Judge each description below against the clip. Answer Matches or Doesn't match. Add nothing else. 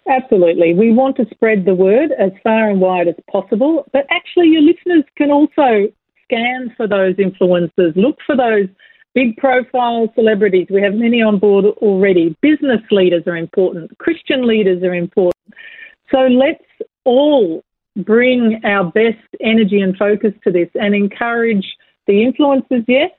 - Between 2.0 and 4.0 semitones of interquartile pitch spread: Doesn't match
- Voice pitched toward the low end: Doesn't match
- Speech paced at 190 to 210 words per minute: Doesn't match